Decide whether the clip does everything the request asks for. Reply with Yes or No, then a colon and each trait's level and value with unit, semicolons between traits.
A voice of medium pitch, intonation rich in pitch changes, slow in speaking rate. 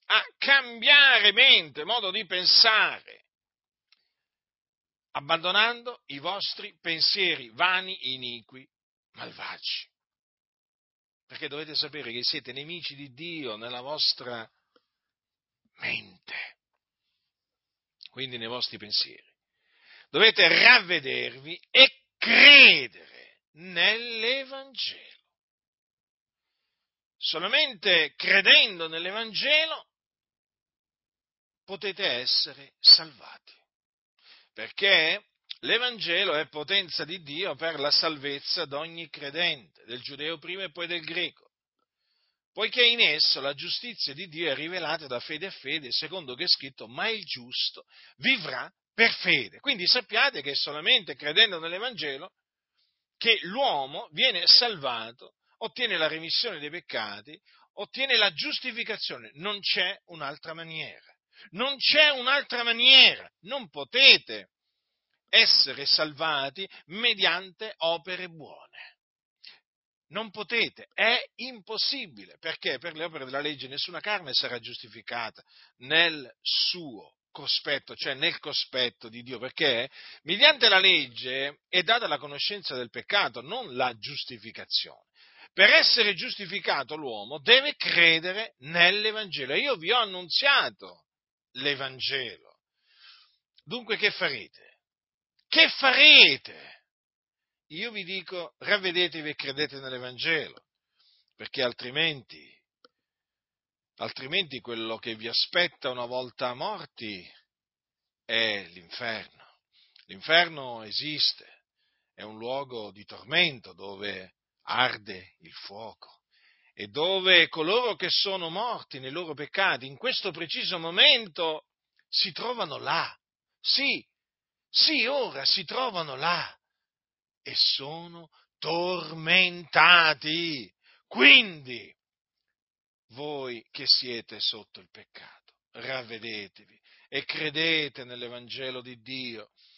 Yes: medium, 165 Hz; wide, 7.2 semitones; slow, 100 wpm